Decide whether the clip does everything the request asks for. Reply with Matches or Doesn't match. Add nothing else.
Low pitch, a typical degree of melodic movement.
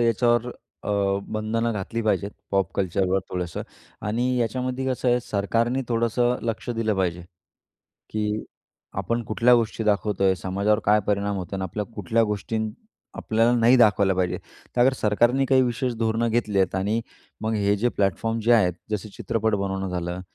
Matches